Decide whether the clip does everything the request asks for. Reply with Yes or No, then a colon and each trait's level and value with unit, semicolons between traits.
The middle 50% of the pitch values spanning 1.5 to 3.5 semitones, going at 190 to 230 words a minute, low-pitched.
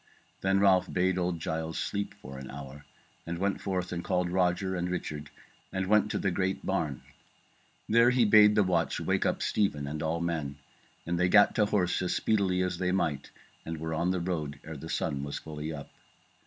Yes: average, 3.2 semitones; average, 200 wpm; very low, 90 Hz